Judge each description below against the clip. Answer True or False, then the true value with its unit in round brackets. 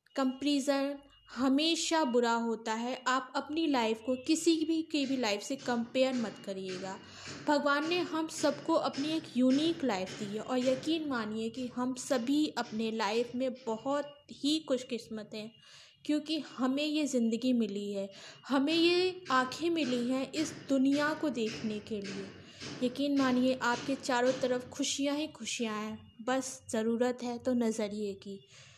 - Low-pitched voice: False (255 Hz)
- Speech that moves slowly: False (150 wpm)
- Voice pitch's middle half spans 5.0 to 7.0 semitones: False (4.0 semitones)